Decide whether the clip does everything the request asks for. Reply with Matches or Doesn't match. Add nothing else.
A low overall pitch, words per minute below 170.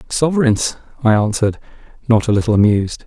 Matches